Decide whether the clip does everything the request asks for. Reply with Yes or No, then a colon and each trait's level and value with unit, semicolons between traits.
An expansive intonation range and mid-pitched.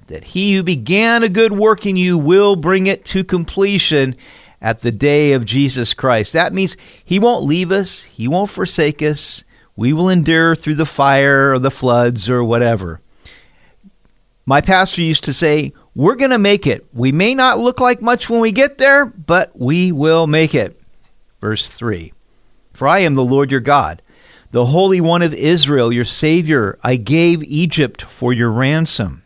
Yes: wide, 6.4 semitones; medium, 155 Hz